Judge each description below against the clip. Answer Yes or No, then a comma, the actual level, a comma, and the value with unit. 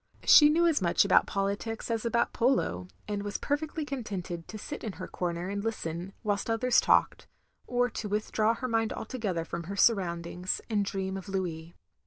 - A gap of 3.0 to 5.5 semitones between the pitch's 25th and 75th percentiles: Yes, average, 4.2 semitones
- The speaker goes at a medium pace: Yes, average, 180 wpm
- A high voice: Yes, high, 205 Hz